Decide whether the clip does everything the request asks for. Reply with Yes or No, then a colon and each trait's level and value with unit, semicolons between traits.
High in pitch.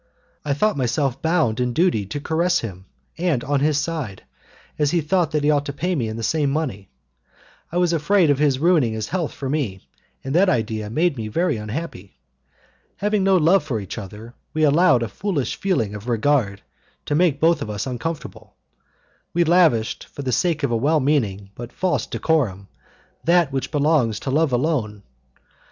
No: medium, 145 Hz